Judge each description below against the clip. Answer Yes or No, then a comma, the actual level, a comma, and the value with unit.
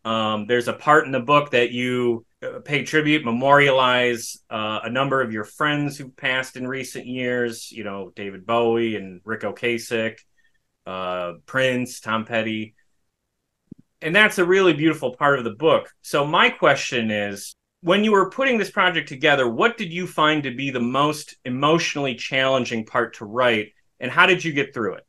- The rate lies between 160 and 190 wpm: Yes, average, 175 wpm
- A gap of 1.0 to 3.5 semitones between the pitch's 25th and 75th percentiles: No, average, 4.9 semitones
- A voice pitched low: Yes, low, 125 Hz